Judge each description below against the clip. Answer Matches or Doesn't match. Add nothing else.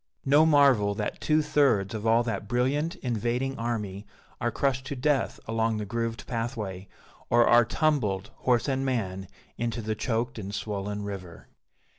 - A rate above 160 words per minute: Doesn't match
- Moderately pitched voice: Doesn't match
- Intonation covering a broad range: Doesn't match